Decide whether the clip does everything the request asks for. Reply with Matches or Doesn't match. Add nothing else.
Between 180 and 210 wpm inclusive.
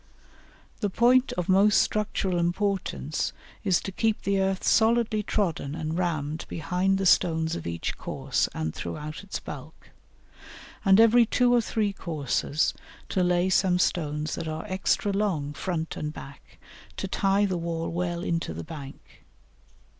Doesn't match